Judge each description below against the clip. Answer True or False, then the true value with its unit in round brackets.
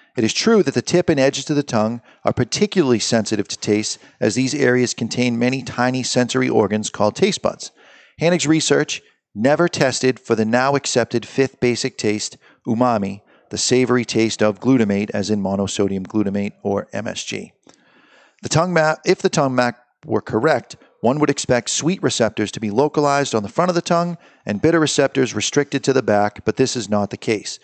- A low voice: True (125 Hz)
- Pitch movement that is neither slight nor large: True (4.9 semitones)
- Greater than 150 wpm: True (185 wpm)